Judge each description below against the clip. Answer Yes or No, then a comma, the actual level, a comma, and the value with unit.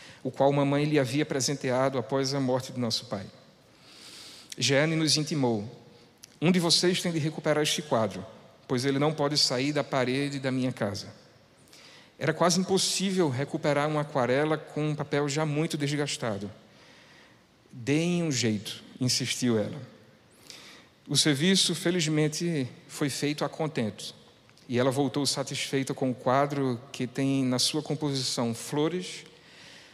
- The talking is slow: No, average, 140 wpm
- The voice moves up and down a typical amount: Yes, average, 3.2 semitones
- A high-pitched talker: No, medium, 140 Hz